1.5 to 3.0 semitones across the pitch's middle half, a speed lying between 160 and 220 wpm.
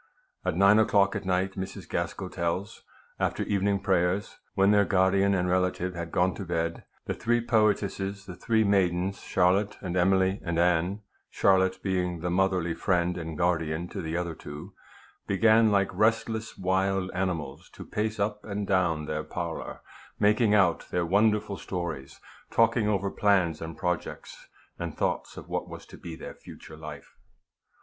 Yes: narrow, 2.5 semitones; average, 170 wpm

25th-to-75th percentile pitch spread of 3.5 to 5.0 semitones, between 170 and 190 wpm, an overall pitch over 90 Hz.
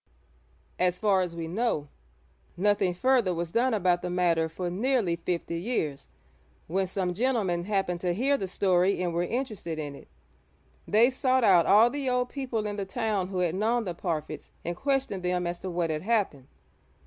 Yes: average, 4.7 semitones; average, 185 wpm; medium, 185 Hz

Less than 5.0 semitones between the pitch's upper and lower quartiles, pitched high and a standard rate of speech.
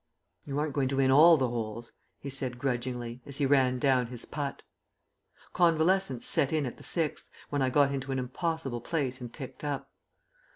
No: narrow, 2.6 semitones; low, 135 Hz; average, 190 wpm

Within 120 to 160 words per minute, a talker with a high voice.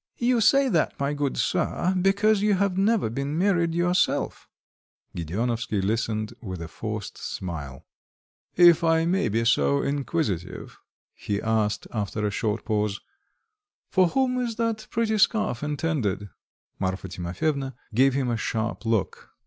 No: average, 140 wpm; low, 135 Hz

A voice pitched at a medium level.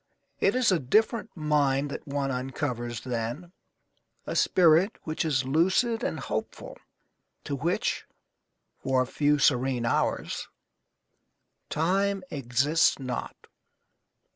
Yes: medium, 145 Hz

